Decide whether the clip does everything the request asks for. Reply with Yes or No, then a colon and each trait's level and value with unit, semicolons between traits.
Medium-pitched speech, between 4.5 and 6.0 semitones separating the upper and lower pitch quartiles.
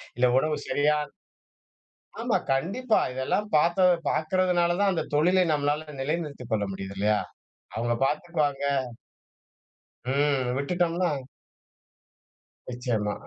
Yes: medium, 150 Hz; wide, 5.4 semitones